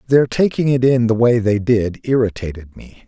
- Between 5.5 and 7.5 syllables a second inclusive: No, 5.0 syllables/s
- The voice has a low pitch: Yes, low, 115 Hz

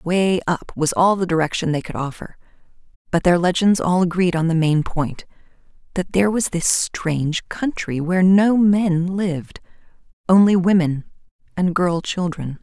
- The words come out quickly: No, average, 145 wpm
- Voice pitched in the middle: Yes, medium, 175 Hz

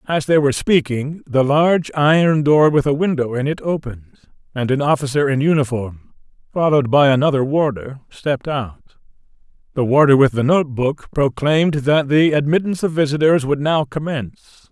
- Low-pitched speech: No, medium, 145 Hz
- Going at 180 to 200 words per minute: No, average, 160 wpm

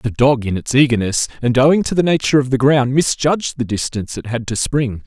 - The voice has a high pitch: No, low, 130 Hz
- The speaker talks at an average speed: No, fast, 235 wpm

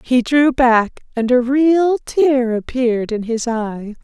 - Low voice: No, very high, 250 Hz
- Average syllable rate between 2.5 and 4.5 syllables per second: Yes, 3.5 syllables/s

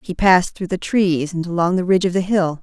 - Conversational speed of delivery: No, fast, 275 wpm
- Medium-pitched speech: Yes, medium, 180 Hz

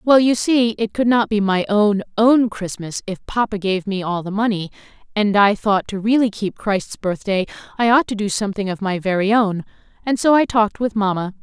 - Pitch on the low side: No, high, 210 Hz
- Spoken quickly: Yes, fast, 215 wpm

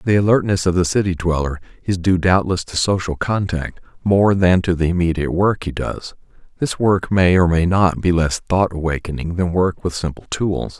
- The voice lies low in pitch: Yes, very low, 90 Hz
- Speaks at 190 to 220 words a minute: Yes, average, 195 wpm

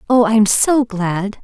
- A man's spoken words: No, female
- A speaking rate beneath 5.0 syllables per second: Yes, 3.3 syllables/s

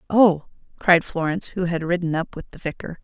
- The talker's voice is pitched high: No, medium, 175 Hz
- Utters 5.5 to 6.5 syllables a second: Yes, 5.7 syllables/s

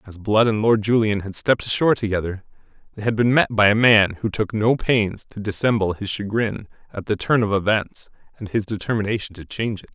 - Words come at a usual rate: No, fast, 210 wpm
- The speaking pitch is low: Yes, low, 105 Hz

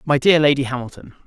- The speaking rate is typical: Yes, average, 190 wpm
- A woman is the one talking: No, male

